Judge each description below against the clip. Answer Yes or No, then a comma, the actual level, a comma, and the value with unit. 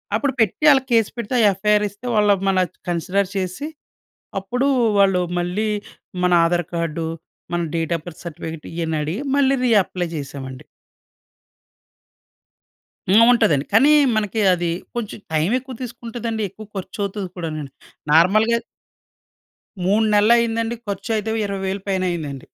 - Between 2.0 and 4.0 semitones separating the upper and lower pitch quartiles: No, average, 4.5 semitones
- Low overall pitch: No, high, 195 Hz